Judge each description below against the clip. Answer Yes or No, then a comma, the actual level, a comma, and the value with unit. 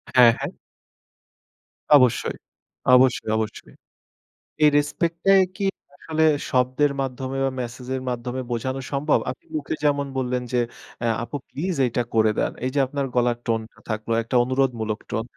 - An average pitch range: Yes, average, 3.0 semitones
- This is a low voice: Yes, low, 130 Hz